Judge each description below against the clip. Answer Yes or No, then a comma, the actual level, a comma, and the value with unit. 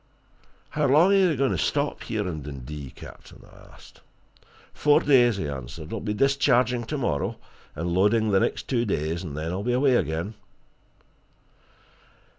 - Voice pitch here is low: Yes, low, 110 Hz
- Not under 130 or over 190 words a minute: Yes, average, 160 wpm